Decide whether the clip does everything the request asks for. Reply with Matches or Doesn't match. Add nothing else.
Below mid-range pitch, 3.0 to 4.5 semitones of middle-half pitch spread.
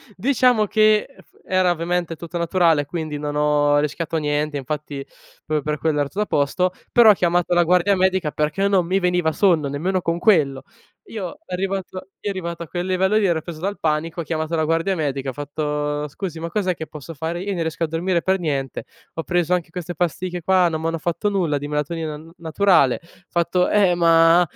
Doesn't match